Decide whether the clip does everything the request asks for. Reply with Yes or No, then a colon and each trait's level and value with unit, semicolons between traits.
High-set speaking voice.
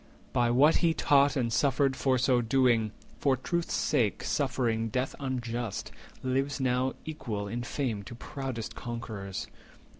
No: low, 125 Hz